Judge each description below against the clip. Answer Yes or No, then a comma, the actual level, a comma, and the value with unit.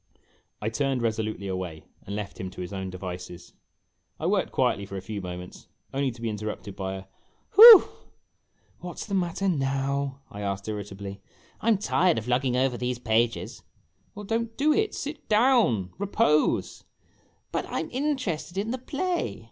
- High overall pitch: No, low, 125 Hz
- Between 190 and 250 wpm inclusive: No, average, 180 wpm